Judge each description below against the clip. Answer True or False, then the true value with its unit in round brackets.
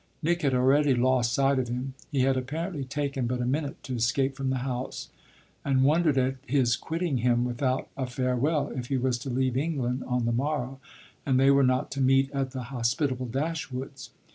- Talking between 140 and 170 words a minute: False (195 wpm)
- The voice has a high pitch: False (130 Hz)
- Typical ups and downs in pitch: False (1.8 semitones)